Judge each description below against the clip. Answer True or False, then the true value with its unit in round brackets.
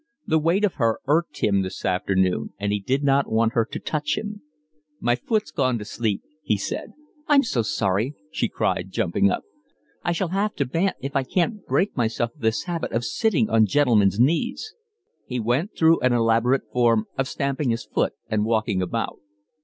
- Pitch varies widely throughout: True (6.5 semitones)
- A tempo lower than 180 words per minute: False (190 wpm)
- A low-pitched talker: True (125 Hz)